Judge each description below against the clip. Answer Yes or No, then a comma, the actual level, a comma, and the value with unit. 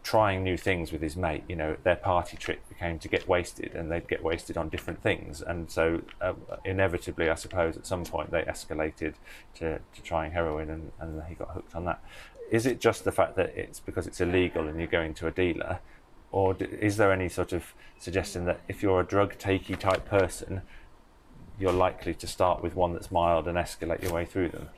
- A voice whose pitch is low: Yes, very low, 90 Hz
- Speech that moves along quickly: Yes, fast, 220 wpm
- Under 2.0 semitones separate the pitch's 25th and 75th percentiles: No, narrow, 2.4 semitones